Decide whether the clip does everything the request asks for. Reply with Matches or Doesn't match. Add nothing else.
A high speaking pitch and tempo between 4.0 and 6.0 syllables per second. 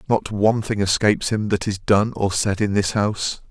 Doesn't match